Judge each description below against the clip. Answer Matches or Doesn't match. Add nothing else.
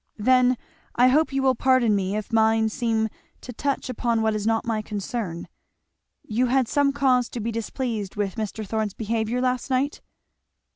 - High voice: Matches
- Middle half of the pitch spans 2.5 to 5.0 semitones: Matches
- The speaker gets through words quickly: Doesn't match